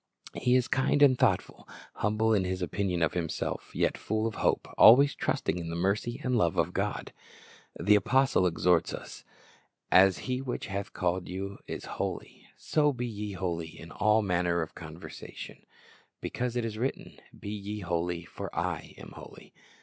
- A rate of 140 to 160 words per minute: No, average, 170 wpm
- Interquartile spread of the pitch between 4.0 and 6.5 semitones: Yes, average, 5.0 semitones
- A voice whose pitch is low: Yes, low, 100 Hz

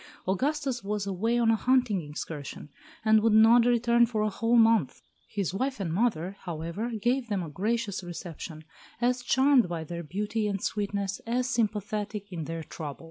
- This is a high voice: Yes, high, 210 Hz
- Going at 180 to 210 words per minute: No, average, 170 wpm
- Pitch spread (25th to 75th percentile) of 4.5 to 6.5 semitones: Yes, average, 4.8 semitones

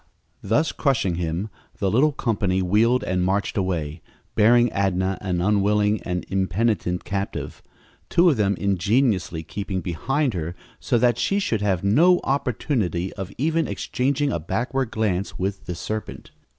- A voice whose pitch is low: Yes, low, 100 Hz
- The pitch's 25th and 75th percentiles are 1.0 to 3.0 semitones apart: No, average, 4.8 semitones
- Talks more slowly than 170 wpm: Yes, average, 145 wpm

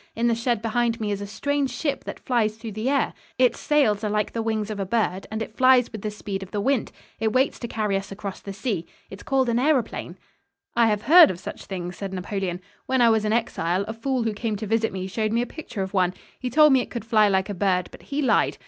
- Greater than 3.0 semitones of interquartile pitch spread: Yes, average, 3.5 semitones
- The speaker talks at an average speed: No, fast, 265 wpm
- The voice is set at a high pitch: Yes, high, 220 Hz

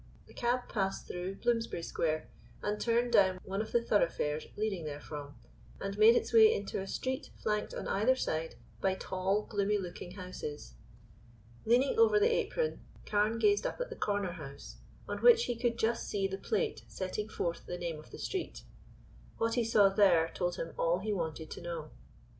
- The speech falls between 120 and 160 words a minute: No, average, 180 wpm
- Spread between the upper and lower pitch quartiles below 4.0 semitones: No, average, 4.8 semitones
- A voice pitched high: Yes, high, 200 Hz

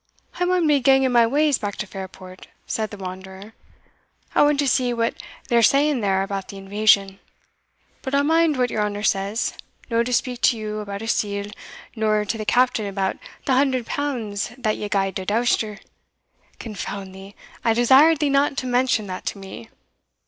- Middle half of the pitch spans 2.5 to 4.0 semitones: No, average, 4.6 semitones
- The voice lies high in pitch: Yes, high, 220 Hz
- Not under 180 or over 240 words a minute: Yes, average, 185 wpm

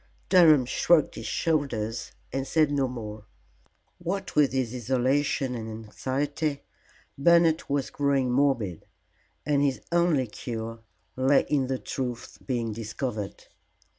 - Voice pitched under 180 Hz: Yes, low, 135 Hz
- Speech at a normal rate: No, slow, 120 wpm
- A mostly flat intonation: No, average, 3.5 semitones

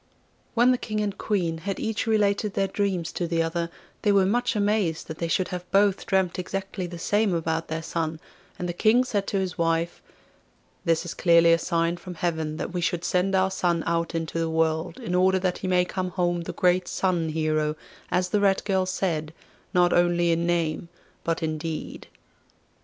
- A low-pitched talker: No, medium, 175 Hz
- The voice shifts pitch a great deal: No, narrow, 2.6 semitones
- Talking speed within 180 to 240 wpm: Yes, average, 200 wpm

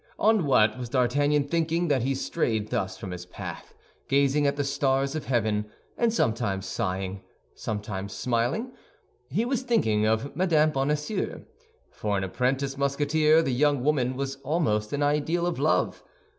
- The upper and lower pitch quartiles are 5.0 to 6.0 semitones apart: Yes, wide, 5.5 semitones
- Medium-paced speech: Yes, average, 155 wpm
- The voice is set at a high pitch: No, low, 135 Hz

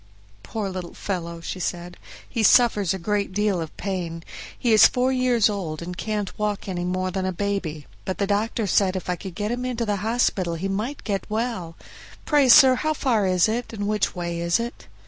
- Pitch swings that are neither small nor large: Yes, average, 3.9 semitones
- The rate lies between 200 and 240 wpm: Yes, fast, 205 wpm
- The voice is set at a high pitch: Yes, high, 200 Hz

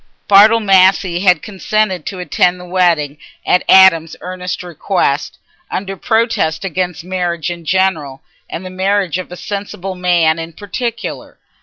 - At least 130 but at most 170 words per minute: Yes, average, 140 wpm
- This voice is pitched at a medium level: Yes, medium, 180 Hz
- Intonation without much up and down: Yes, narrow, 2.2 semitones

